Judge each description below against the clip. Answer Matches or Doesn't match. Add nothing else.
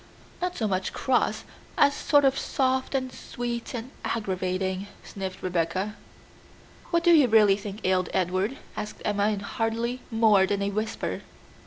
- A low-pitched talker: Doesn't match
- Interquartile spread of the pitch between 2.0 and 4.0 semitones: Doesn't match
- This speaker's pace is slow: Doesn't match